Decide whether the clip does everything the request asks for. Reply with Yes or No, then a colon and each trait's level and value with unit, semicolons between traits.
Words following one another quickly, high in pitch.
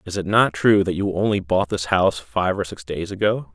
No: fast, 255 wpm; very low, 95 Hz